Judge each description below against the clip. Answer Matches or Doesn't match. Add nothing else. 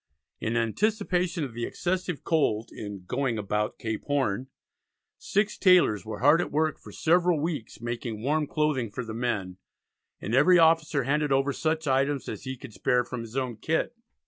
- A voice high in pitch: Doesn't match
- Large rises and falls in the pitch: Matches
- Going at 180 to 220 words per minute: Doesn't match